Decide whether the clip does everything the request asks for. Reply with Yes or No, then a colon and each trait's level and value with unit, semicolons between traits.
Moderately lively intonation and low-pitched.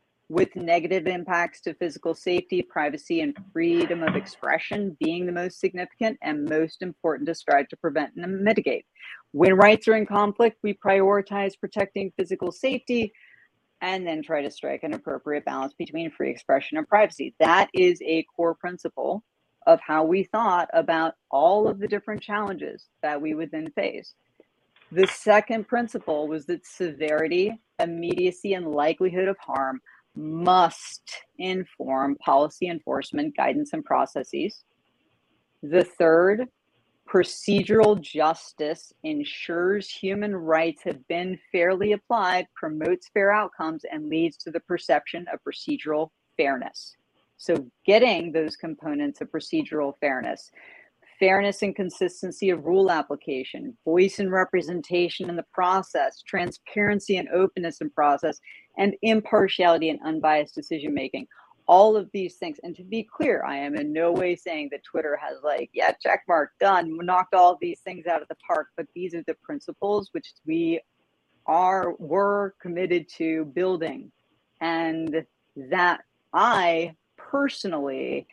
No: average, 4.1 semitones; medium, 180 Hz